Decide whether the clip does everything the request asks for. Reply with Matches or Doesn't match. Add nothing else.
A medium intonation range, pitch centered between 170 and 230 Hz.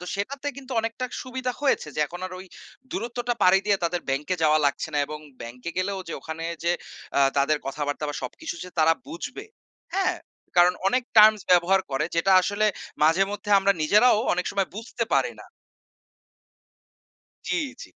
Doesn't match